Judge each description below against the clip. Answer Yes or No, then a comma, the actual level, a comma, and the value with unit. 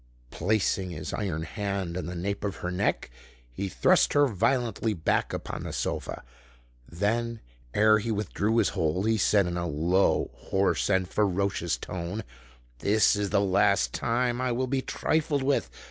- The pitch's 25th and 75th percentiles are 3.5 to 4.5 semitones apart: Yes, average, 3.8 semitones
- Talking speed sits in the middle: Yes, average, 160 wpm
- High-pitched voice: No, low, 100 Hz